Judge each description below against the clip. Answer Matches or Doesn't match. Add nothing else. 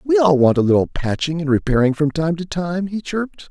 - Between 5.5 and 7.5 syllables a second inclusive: Matches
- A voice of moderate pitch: Matches